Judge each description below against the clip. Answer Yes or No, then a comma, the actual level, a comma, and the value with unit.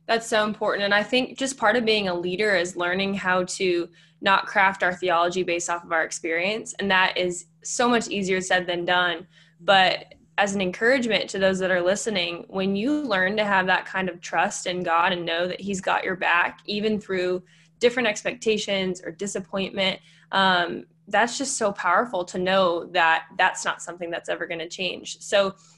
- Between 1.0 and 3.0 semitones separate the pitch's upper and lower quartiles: Yes, average, 2.7 semitones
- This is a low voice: No, medium, 185 Hz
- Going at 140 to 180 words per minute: No, average, 195 wpm